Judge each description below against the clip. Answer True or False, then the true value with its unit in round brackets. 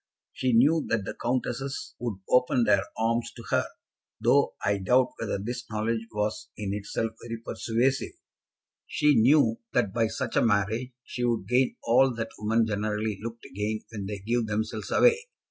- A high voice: False (115 Hz)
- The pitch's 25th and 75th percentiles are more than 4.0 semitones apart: False (2.5 semitones)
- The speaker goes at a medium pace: True (170 wpm)